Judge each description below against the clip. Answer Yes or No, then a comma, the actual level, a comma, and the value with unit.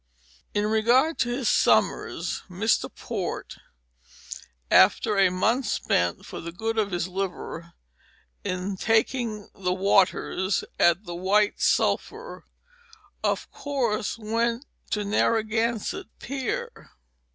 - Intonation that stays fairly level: No, average, 3.7 semitones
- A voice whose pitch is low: No, high, 210 Hz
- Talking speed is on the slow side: Yes, slow, 110 wpm